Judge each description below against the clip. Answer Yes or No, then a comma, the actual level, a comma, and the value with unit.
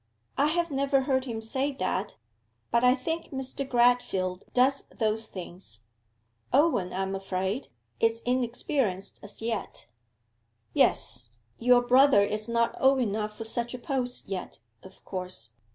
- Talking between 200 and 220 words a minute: No, average, 140 wpm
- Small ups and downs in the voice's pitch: No, average, 5.2 semitones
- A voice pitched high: Yes, high, 235 Hz